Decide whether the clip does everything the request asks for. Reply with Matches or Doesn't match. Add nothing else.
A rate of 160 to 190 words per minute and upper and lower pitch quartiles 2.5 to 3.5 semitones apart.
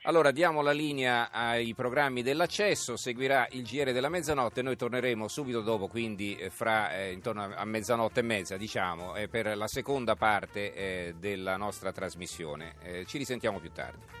Doesn't match